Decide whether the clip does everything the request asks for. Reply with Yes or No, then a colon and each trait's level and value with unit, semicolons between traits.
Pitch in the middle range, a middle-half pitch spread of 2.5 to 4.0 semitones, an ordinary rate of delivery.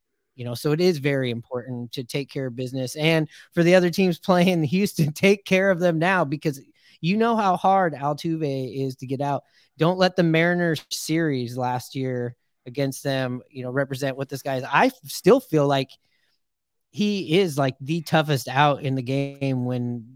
No: medium, 145 Hz; average, 4.4 semitones; average, 195 wpm